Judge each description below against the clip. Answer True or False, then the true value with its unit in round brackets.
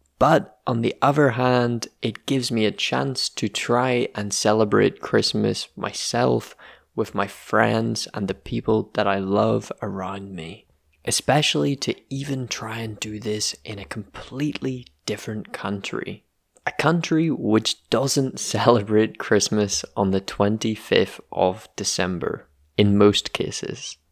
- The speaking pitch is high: False (110 Hz)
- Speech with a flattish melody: False (3.6 semitones)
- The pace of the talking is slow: True (130 wpm)